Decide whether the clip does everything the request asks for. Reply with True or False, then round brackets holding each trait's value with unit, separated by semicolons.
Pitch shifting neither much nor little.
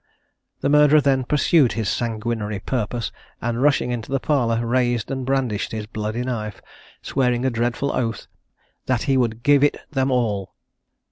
True (3.0 semitones)